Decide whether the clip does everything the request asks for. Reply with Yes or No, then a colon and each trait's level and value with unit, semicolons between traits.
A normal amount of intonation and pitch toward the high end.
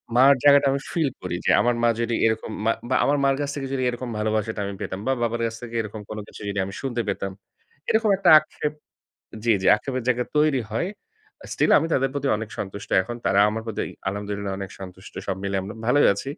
No: average, 4.9 semitones; low, 115 Hz